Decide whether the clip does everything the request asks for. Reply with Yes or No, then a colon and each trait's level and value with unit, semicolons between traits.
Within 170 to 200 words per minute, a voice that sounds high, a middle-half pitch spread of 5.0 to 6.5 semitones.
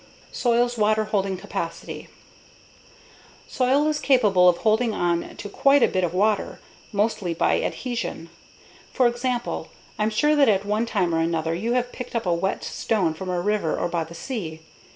Yes: average, 175 wpm; high, 210 Hz; wide, 5.4 semitones